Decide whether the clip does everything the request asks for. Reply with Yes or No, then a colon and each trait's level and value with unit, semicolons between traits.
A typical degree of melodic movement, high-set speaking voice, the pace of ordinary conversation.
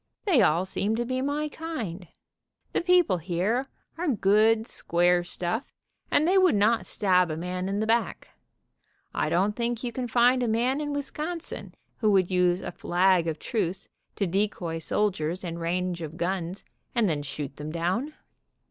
No: wide, 5.7 semitones; high, 200 Hz; average, 170 wpm